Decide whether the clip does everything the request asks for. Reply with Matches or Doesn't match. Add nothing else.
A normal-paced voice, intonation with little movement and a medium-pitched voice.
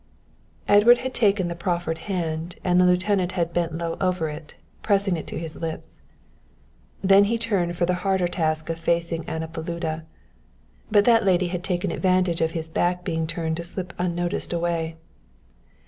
Matches